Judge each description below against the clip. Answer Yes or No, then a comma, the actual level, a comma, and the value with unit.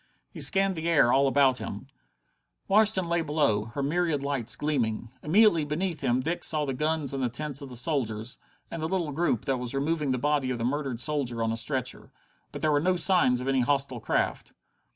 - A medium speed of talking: No, fast, 210 wpm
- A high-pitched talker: No, medium, 140 Hz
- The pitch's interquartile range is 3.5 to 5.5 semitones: Yes, average, 4.1 semitones